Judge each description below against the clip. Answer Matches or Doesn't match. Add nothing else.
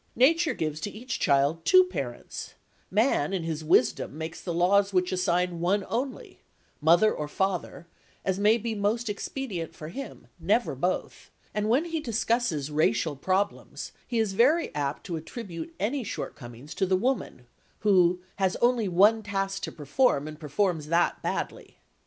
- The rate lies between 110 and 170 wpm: Matches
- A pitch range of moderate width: Doesn't match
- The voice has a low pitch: Doesn't match